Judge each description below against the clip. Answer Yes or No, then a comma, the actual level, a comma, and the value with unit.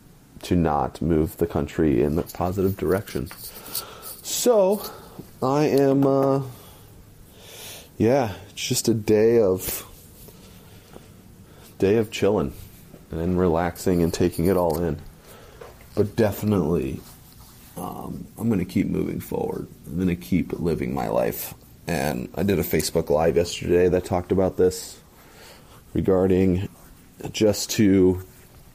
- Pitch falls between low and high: No, very low, 95 Hz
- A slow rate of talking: Yes, slow, 125 wpm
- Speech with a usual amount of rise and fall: Yes, average, 3.6 semitones